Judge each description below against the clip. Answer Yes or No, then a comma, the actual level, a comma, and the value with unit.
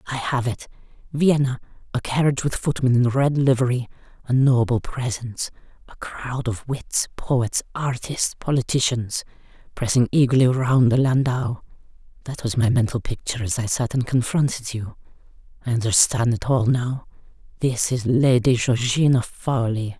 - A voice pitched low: Yes, low, 125 Hz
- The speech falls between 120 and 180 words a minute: Yes, slow, 135 wpm